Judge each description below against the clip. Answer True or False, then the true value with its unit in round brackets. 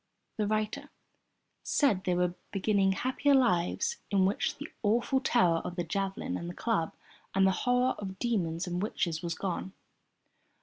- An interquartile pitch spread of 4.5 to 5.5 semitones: True (5.0 semitones)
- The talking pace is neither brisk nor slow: True (160 wpm)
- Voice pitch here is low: False (195 Hz)